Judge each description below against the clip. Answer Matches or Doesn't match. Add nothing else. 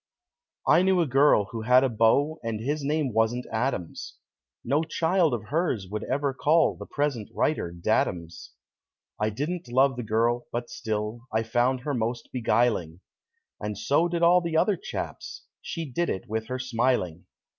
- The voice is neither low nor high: Doesn't match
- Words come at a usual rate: Matches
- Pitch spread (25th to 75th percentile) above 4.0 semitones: Matches